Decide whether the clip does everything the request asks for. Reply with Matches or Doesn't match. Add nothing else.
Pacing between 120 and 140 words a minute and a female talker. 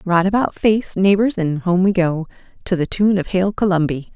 Doesn't match